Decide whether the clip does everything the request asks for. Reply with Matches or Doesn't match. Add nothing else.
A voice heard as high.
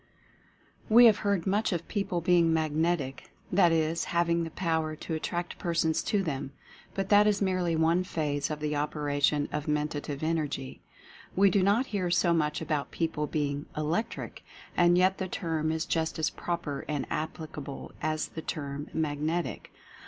Doesn't match